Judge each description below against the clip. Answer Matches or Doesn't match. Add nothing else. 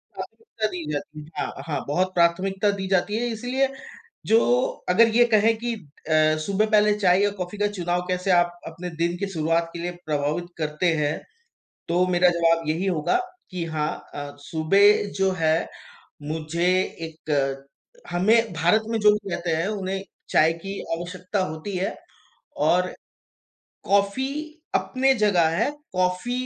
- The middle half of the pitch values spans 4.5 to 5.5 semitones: Doesn't match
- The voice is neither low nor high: Matches